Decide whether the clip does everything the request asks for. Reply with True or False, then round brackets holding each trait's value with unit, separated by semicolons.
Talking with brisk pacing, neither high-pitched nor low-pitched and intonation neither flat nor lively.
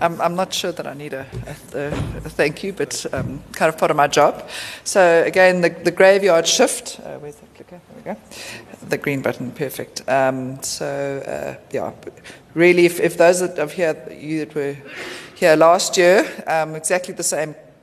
False (185 wpm; 160 Hz; 3.5 semitones)